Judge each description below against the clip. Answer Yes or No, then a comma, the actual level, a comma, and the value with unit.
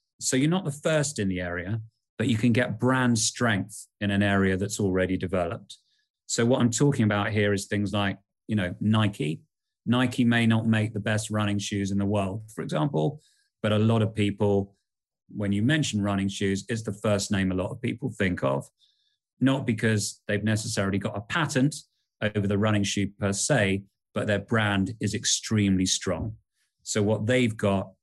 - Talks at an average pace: Yes, average, 190 wpm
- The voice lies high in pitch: No, low, 105 Hz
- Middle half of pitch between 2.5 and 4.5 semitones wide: Yes, average, 3.1 semitones